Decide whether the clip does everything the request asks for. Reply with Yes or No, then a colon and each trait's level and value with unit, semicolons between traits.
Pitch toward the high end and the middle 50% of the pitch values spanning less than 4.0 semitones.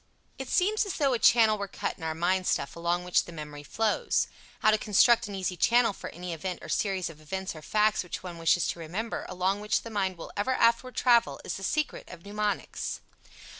No: high, 195 Hz; average, 4.3 semitones